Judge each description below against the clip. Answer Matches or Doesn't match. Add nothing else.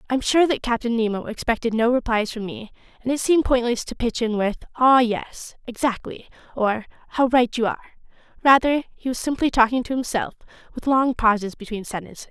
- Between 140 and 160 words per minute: Doesn't match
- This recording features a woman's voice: Matches